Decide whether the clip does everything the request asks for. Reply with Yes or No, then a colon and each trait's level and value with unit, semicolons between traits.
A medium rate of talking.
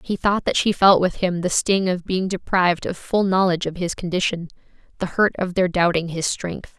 No: fast, 220 wpm